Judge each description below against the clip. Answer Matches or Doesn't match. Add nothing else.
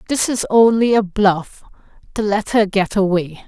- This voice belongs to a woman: Matches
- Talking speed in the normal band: Matches